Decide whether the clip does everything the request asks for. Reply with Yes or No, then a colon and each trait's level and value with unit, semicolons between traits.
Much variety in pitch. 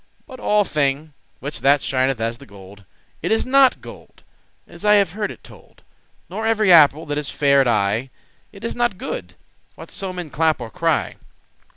Yes: wide, 7.8 semitones